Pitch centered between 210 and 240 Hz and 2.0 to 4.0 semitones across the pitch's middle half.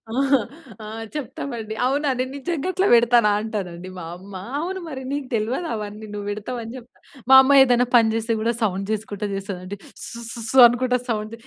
Yes: high, 230 Hz; average, 3.7 semitones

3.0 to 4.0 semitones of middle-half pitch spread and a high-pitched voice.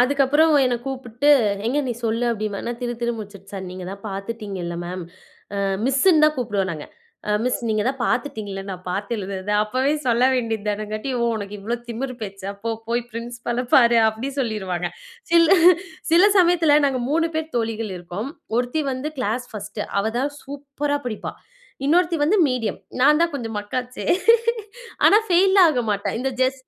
No: average, 4.8 semitones; high, 235 Hz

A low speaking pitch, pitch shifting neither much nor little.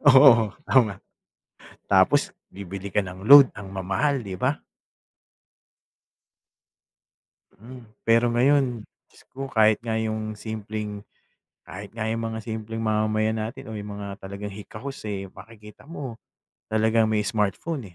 No: low, 110 Hz; narrow, 2.1 semitones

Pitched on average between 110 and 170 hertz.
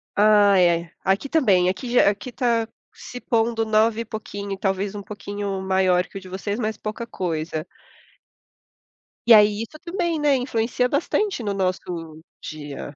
No: high, 210 Hz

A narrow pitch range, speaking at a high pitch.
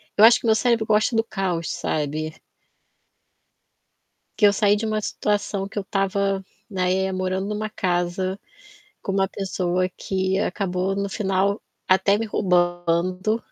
Yes: narrow, 2.2 semitones; high, 195 Hz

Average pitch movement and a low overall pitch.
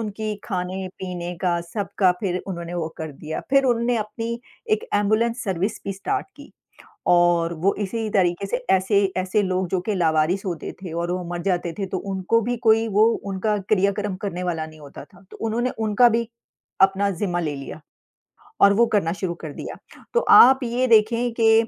No: average, 4.1 semitones; high, 195 Hz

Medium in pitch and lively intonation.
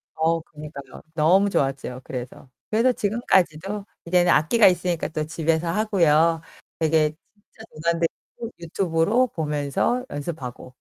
No: medium, 165 Hz; average, 4.2 semitones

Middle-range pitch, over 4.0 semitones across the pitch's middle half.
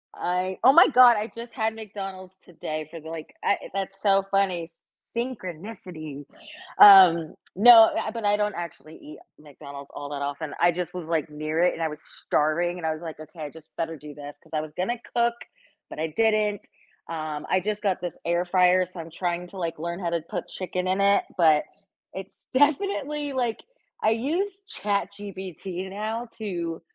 Yes: medium, 180 Hz; average, 4.5 semitones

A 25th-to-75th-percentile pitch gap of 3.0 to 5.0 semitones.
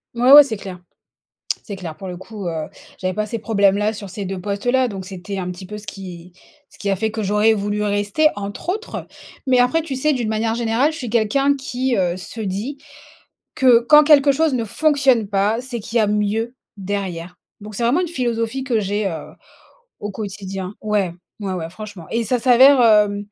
Yes: average, 4.0 semitones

